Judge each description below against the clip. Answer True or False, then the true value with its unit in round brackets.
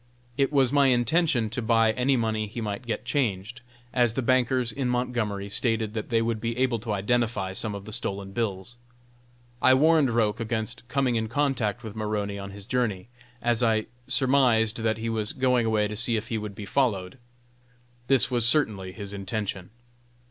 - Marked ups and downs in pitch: False (2.9 semitones)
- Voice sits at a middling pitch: False (115 Hz)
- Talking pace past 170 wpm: True (185 wpm)